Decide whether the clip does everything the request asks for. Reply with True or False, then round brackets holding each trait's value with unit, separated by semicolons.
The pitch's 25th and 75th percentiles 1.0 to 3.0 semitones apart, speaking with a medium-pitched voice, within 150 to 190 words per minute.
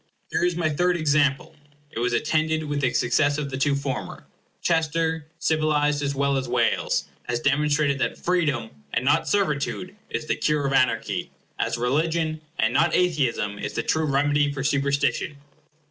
True (2.4 semitones; 145 Hz; 165 wpm)